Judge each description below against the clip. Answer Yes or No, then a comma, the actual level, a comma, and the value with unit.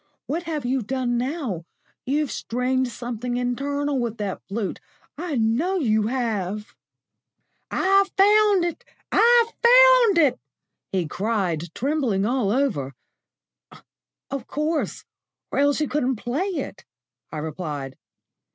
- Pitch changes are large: Yes, wide, 6.4 semitones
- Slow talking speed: Yes, slow, 120 wpm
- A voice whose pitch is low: No, very high, 255 Hz